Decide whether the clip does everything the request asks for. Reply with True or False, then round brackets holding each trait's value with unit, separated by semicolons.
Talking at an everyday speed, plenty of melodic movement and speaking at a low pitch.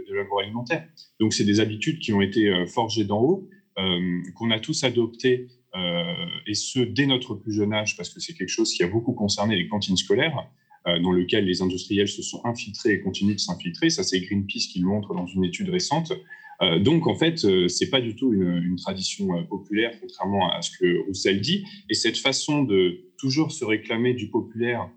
True (210 wpm; 8.1 semitones; 115 Hz)